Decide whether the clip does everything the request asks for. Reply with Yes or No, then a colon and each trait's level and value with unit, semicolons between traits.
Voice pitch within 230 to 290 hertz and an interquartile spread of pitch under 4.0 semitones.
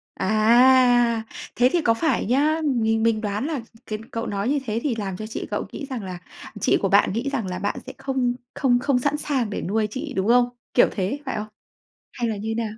Yes: high, 235 Hz; average, 3.6 semitones